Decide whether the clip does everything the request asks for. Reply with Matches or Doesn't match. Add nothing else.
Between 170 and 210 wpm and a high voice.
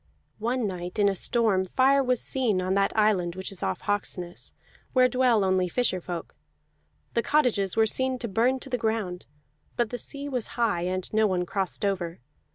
Matches